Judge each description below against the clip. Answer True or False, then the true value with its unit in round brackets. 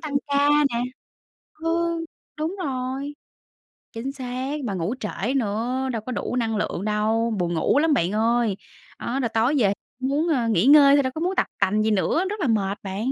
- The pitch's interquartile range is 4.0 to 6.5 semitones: True (4.8 semitones)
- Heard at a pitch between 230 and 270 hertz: True (245 Hz)